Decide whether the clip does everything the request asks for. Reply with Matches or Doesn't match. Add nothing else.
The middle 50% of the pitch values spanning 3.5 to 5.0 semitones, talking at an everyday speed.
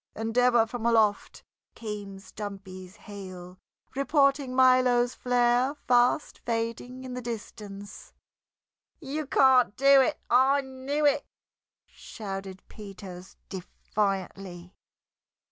Doesn't match